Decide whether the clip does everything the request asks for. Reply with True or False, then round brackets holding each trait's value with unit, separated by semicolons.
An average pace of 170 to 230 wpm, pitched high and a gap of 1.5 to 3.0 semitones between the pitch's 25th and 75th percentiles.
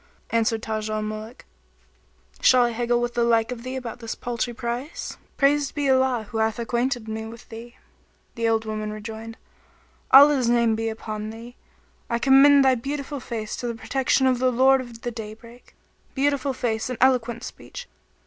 True (175 wpm; 235 Hz; 2.6 semitones)